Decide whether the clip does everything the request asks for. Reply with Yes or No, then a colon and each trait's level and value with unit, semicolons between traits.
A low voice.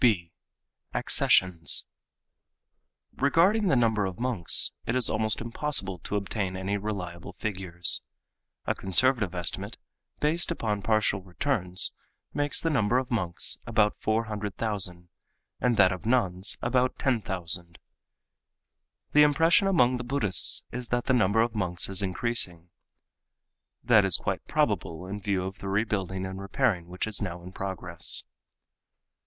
Yes: low, 105 Hz